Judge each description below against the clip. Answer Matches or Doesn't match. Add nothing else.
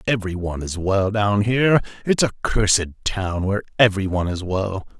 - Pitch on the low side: Matches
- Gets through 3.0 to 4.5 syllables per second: Doesn't match